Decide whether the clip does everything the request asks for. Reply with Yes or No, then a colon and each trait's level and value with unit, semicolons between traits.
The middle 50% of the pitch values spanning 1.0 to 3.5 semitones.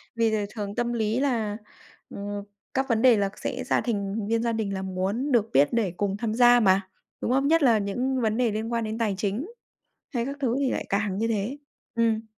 Yes: average, 3.1 semitones